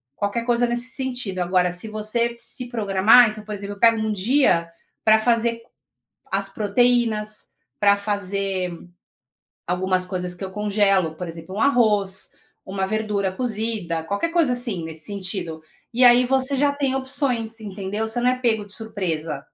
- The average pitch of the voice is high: Yes, high, 210 Hz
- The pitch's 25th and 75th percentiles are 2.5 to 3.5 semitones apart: No, average, 4.0 semitones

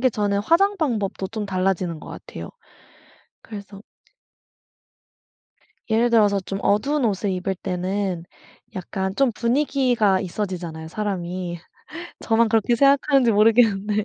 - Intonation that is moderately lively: Yes, average, 3.6 semitones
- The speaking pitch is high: Yes, high, 205 Hz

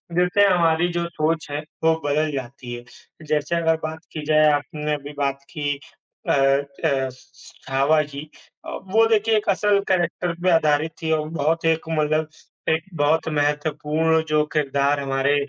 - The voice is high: No, medium, 155 Hz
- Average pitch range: No, narrow, 2.1 semitones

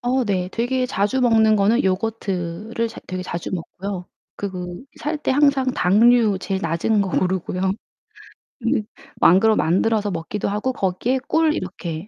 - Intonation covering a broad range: No, average, 4.5 semitones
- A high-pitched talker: Yes, high, 205 Hz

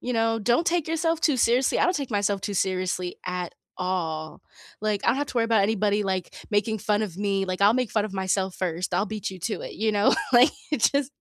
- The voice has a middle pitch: No, high, 205 Hz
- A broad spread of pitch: No, average, 4.1 semitones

